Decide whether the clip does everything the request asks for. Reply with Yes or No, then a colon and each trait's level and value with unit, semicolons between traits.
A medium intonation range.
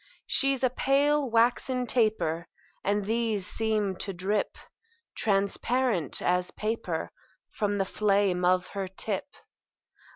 Yes: average, 3.9 semitones